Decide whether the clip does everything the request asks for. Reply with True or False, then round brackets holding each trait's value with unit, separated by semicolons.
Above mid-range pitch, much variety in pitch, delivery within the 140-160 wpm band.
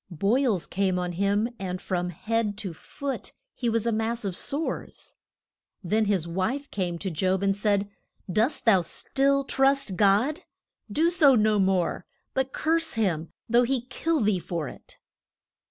True (210 Hz; 5.7 semitones; 155 wpm)